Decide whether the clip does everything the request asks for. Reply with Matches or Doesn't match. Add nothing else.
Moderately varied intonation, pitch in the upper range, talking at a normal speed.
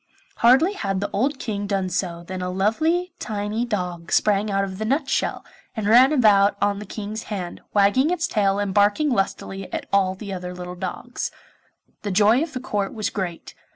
Matches